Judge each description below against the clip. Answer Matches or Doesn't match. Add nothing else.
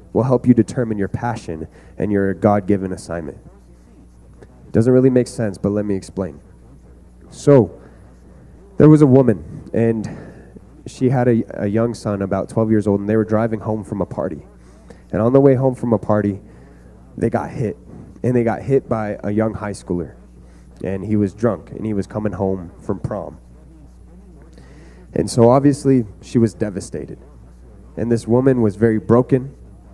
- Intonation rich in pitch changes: Matches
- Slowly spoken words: Doesn't match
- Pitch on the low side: Matches